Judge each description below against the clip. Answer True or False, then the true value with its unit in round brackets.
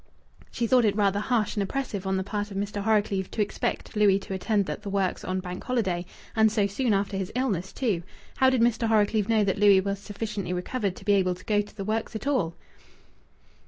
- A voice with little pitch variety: True (2.3 semitones)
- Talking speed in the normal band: False (225 wpm)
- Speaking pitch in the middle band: False (205 Hz)